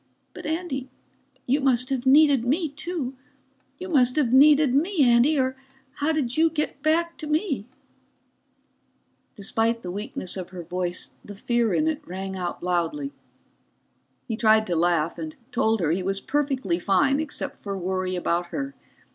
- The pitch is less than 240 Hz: No, very high, 250 Hz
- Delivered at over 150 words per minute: Yes, average, 160 wpm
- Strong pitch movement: Yes, wide, 7.6 semitones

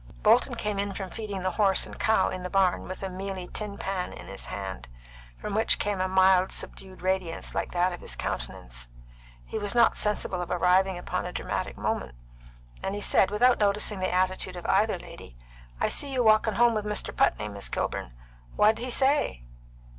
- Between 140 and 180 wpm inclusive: No, average, 195 wpm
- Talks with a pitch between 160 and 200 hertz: Yes, high, 190 Hz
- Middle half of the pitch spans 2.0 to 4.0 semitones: Yes, narrow, 2.6 semitones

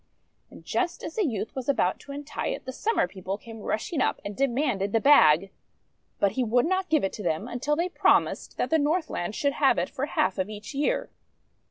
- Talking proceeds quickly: Yes, fast, 220 wpm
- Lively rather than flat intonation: Yes, wide, 6.6 semitones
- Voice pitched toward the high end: Yes, very high, 250 Hz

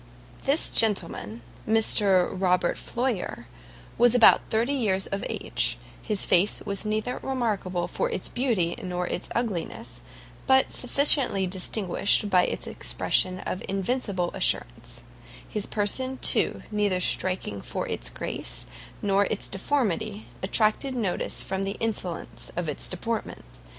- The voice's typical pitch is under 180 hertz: No, high, 200 Hz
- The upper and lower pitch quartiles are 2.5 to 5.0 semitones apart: Yes, average, 4.0 semitones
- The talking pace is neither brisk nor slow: No, slow, 130 wpm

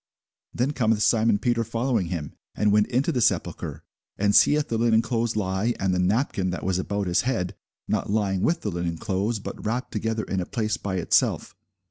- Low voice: Yes, low, 105 Hz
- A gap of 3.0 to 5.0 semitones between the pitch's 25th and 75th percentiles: Yes, average, 3.5 semitones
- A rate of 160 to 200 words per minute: Yes, average, 195 wpm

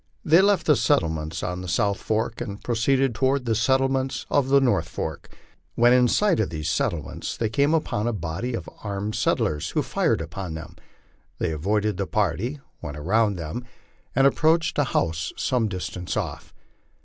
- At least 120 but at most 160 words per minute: No, average, 175 wpm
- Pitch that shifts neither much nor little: No, wide, 7.4 semitones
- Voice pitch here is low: Yes, low, 110 Hz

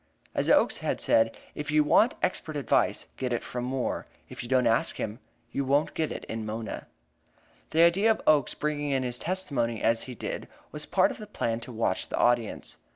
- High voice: No, low, 130 Hz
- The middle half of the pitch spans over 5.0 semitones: No, average, 4.6 semitones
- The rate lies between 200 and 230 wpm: Yes, fast, 205 wpm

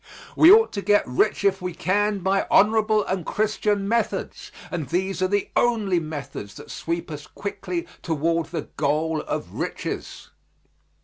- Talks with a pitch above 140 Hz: Yes, high, 190 Hz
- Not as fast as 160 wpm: Yes, average, 150 wpm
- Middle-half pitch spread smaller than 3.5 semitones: No, average, 3.8 semitones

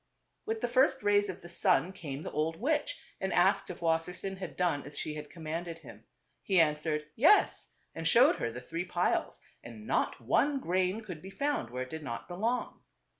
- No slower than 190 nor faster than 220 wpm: Yes, average, 195 wpm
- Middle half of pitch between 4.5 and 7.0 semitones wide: Yes, average, 5.3 semitones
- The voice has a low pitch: No, medium, 175 Hz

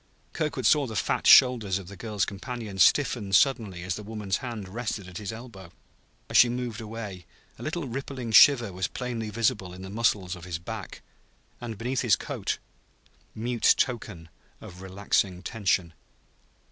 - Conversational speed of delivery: Yes, average, 160 wpm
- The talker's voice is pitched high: No, low, 110 Hz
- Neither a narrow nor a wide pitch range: Yes, average, 4.2 semitones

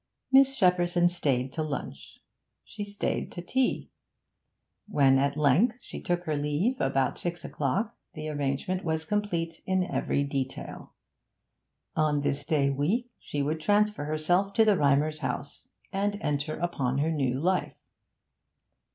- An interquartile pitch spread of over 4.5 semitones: Yes, average, 4.9 semitones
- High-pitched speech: No, medium, 155 Hz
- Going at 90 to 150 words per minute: Yes, average, 140 wpm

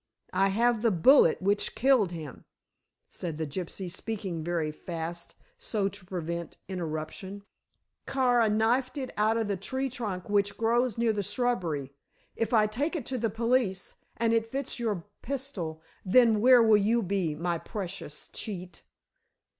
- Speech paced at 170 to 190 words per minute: No, average, 155 wpm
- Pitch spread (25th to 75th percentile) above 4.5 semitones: Yes, average, 5.0 semitones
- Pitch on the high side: Yes, high, 205 Hz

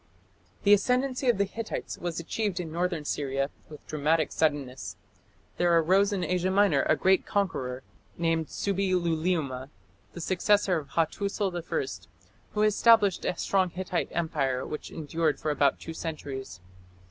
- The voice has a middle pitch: Yes, medium, 170 Hz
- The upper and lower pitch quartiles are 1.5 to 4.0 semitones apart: No, average, 4.4 semitones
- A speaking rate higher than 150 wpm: No, average, 145 wpm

